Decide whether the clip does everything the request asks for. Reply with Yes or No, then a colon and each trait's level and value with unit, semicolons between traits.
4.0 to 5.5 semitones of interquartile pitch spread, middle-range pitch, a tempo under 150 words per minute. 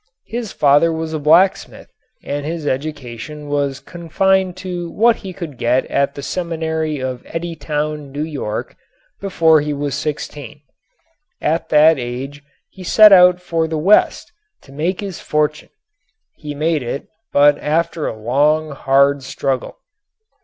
No: average, 3.0 semitones; medium, 150 Hz; average, 140 wpm